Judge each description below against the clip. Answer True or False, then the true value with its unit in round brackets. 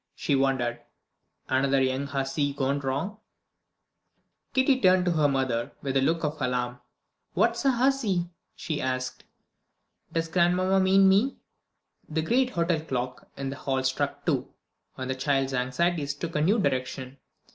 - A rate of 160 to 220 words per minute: False (145 wpm)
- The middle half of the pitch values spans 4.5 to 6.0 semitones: True (5.3 semitones)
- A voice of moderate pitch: True (145 Hz)